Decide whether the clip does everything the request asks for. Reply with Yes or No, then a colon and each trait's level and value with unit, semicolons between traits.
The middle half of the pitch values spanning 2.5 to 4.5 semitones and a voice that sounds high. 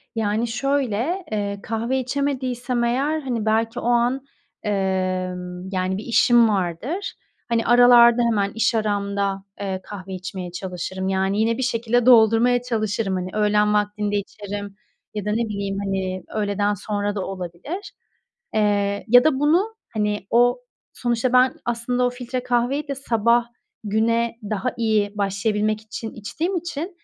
Yes: average, 3.4 semitones; high, 220 Hz